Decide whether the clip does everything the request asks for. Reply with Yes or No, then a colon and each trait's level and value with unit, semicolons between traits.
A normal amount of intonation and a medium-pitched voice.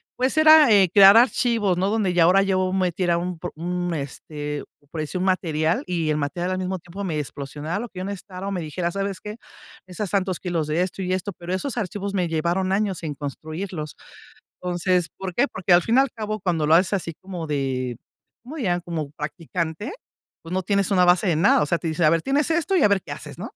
Yes: average, 3.3 semitones; medium, 180 Hz